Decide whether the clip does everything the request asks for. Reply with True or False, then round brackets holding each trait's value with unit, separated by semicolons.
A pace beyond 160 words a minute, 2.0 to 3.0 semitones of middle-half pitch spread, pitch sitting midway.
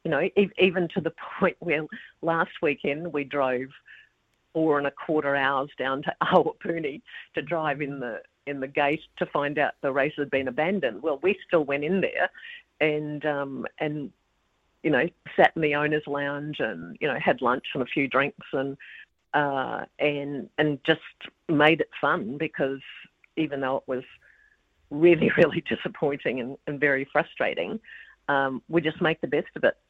True (175 wpm; 2.4 semitones; 145 Hz)